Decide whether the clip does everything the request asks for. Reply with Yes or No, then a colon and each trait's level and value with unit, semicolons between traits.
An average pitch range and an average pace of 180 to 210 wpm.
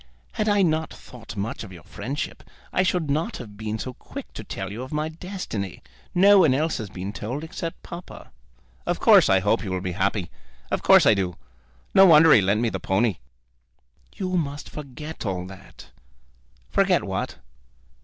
No: wide, 8.3 semitones; average, 185 wpm